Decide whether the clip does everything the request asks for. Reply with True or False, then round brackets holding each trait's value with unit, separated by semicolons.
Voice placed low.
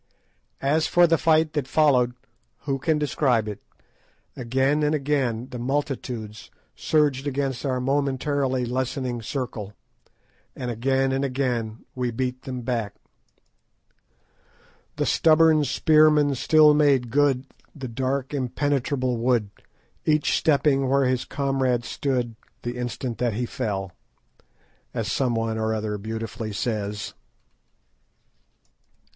True (130 Hz)